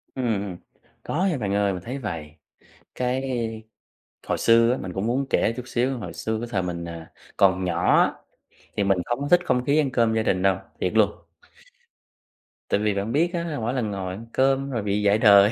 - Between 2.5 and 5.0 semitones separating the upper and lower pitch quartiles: Yes, average, 4.6 semitones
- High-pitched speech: No, low, 110 Hz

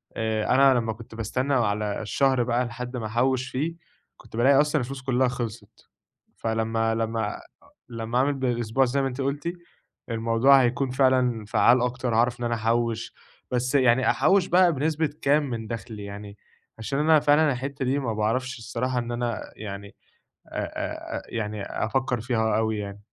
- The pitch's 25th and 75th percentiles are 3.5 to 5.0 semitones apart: No, average, 3.0 semitones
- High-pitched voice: No, low, 120 Hz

